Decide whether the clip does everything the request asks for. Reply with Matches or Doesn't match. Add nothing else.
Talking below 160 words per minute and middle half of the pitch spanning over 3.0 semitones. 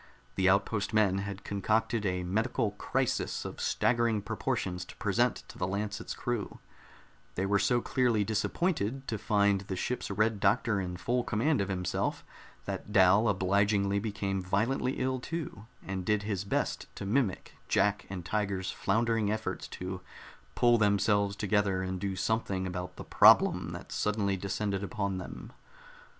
Doesn't match